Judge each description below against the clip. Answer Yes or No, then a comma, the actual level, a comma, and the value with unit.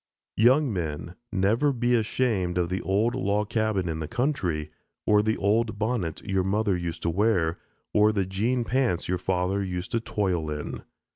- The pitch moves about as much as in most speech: Yes, average, 4.0 semitones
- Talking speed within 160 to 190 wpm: Yes, average, 170 wpm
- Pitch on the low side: Yes, low, 100 Hz